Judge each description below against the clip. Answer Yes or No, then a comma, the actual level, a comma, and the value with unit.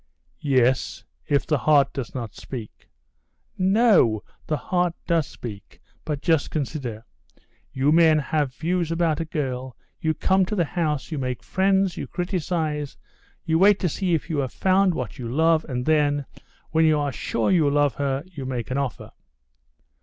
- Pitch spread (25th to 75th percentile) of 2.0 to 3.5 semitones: No, average, 4.2 semitones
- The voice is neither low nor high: Yes, medium, 150 Hz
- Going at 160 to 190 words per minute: Yes, average, 170 wpm